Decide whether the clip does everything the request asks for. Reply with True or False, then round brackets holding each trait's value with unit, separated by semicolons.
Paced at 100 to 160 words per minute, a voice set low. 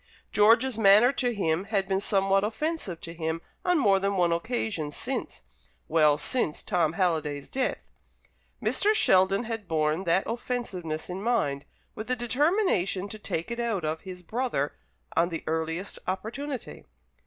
False (150 wpm; 195 Hz)